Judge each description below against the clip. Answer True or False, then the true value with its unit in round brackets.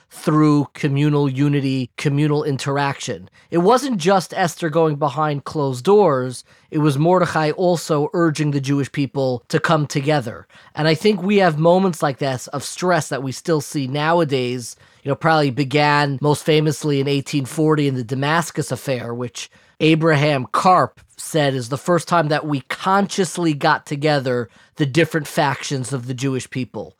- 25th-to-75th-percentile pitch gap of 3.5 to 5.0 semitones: False (2.8 semitones)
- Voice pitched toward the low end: False (150 Hz)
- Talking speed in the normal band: True (160 wpm)